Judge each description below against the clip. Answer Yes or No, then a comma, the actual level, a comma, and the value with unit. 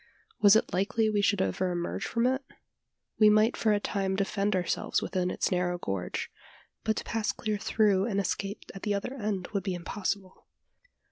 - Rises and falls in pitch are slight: Yes, narrow, 2.3 semitones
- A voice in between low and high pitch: No, high, 200 Hz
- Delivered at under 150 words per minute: No, average, 185 wpm